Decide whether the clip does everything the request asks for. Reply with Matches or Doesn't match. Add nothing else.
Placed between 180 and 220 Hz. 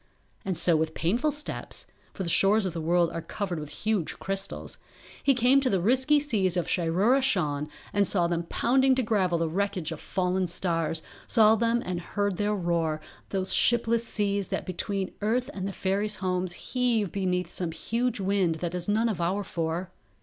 Matches